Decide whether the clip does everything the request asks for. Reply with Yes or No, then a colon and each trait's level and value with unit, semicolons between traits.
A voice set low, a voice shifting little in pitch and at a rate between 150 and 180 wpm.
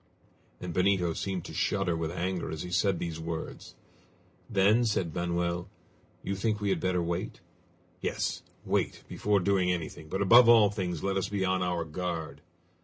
Yes: very low, 90 Hz; narrow, 2.3 semitones; average, 170 wpm